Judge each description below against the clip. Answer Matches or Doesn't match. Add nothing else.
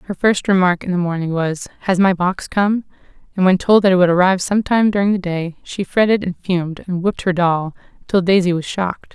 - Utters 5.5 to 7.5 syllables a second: Matches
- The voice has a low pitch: Doesn't match